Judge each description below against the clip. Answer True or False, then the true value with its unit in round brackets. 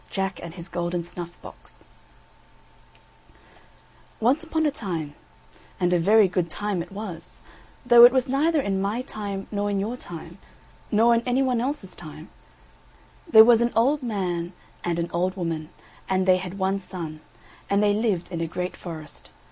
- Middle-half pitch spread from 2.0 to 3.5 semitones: False (5.0 semitones)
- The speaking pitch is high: True (195 Hz)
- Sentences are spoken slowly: False (170 wpm)